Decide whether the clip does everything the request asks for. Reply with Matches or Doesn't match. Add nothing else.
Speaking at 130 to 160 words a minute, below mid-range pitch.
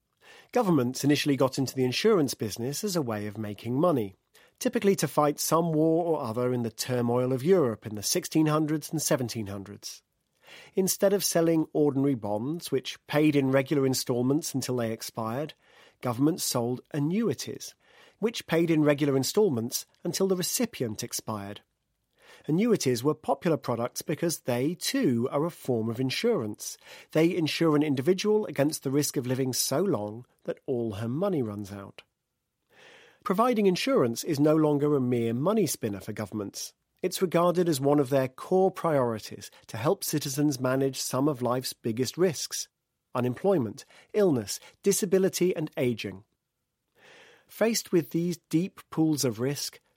Doesn't match